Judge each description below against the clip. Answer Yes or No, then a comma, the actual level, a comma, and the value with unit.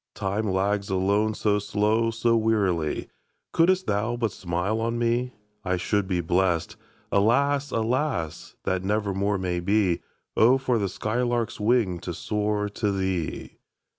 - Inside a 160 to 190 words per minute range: No, average, 145 wpm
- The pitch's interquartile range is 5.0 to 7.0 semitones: No, average, 3.4 semitones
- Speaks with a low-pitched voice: Yes, low, 105 Hz